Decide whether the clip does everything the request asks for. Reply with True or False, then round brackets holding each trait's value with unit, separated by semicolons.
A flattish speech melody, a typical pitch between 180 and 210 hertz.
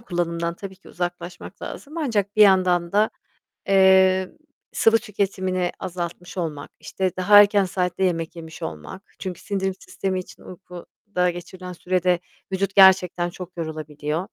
True (1.8 semitones; 185 Hz)